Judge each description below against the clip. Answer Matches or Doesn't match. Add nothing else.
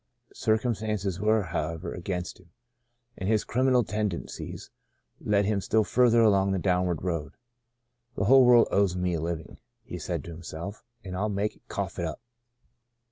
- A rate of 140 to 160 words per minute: Doesn't match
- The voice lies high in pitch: Doesn't match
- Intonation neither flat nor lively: Matches